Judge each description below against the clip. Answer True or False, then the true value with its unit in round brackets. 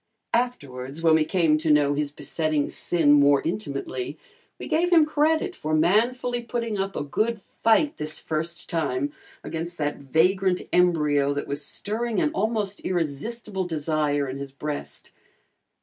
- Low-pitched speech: False (165 Hz)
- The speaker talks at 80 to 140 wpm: False (150 wpm)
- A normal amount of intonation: False (6.9 semitones)